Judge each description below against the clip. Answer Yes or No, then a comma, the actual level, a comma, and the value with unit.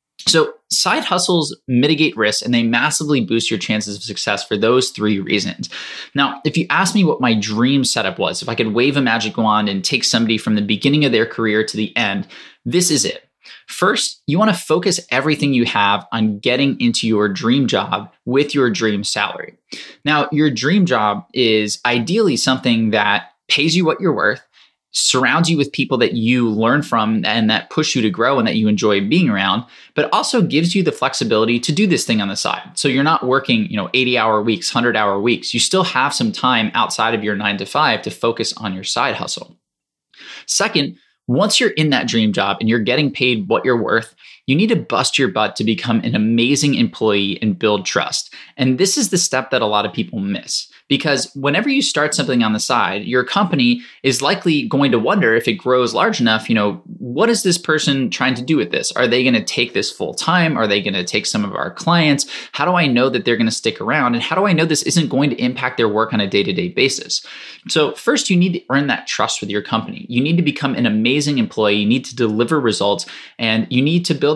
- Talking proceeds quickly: Yes, fast, 230 wpm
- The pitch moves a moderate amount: No, wide, 6.0 semitones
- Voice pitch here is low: Yes, low, 125 Hz